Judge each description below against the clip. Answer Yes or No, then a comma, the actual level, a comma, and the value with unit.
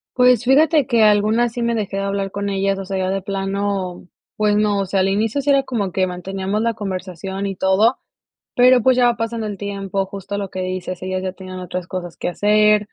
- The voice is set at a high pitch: Yes, high, 200 Hz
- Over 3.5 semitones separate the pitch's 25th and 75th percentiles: No, average, 2.7 semitones